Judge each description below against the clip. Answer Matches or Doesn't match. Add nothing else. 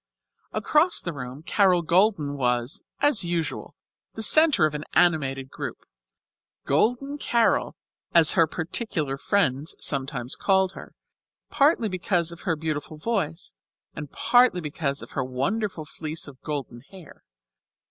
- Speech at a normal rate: Doesn't match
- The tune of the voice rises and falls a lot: Matches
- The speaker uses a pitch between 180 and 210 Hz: Doesn't match